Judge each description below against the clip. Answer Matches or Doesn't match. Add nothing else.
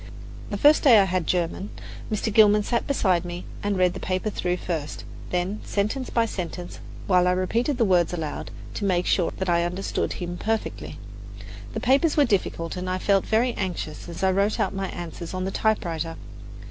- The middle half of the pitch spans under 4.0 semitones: Matches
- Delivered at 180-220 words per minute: Matches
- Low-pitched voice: Doesn't match